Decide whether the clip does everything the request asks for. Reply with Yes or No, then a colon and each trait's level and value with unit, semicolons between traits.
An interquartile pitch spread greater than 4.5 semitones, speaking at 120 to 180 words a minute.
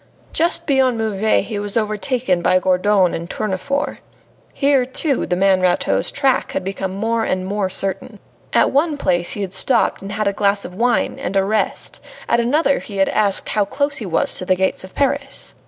No: average, 5.3 semitones; average, 190 wpm